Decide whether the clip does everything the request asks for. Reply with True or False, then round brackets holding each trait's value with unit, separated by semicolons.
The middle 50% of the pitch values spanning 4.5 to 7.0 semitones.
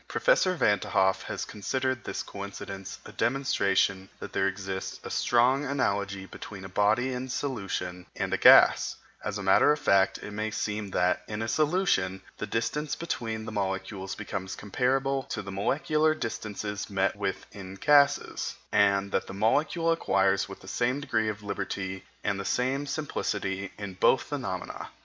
True (5.3 semitones)